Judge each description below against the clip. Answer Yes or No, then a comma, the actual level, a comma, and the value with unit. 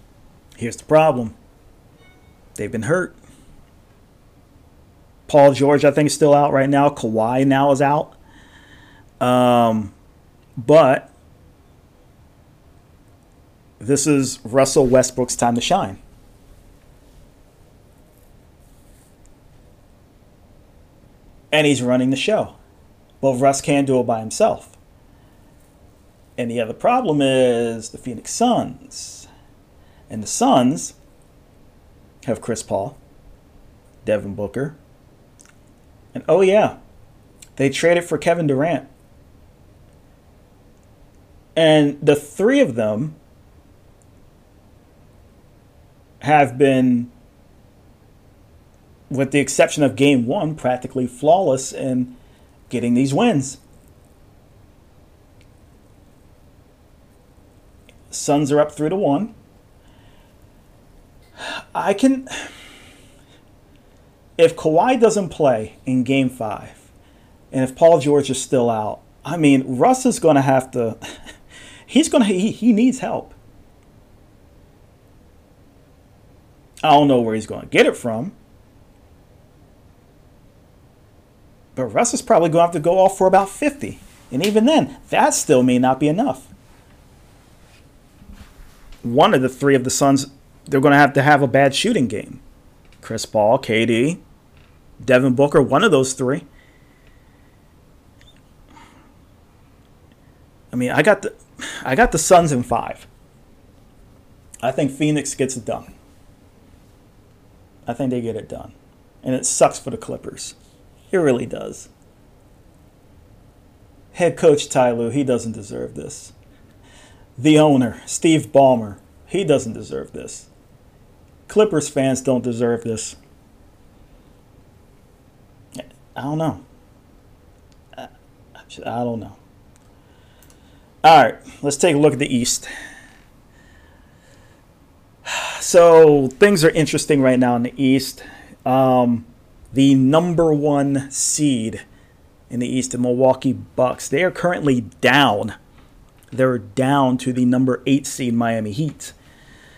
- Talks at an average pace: No, slow, 110 wpm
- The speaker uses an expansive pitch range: Yes, wide, 6.2 semitones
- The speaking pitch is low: Yes, low, 125 Hz